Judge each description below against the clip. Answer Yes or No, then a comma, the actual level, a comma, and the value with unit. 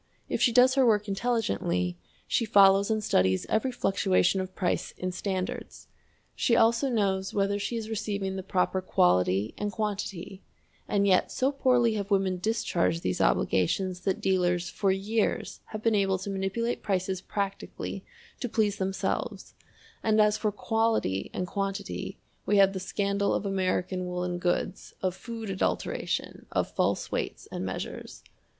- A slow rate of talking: No, average, 155 wpm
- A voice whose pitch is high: Yes, high, 195 Hz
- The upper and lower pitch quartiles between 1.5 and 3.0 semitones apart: Yes, average, 2.7 semitones